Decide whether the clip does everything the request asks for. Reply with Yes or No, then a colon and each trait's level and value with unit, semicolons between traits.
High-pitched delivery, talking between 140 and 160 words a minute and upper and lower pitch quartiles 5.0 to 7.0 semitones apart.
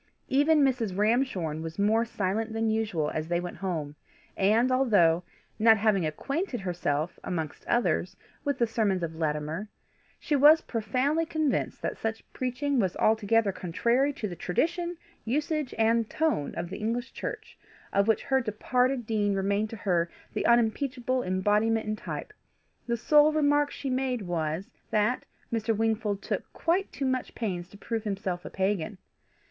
Yes: high, 220 Hz; average, 155 wpm; average, 5.3 semitones